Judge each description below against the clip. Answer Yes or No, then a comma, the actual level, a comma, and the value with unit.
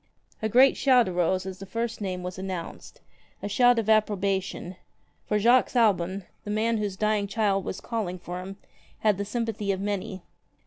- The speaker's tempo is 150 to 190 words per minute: Yes, average, 180 wpm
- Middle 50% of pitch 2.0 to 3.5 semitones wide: Yes, average, 2.8 semitones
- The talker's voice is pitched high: Yes, high, 205 Hz